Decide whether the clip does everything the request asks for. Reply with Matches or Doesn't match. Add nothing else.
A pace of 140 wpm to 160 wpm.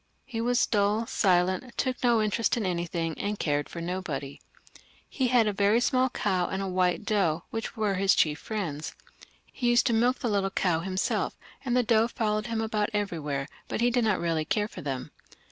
Doesn't match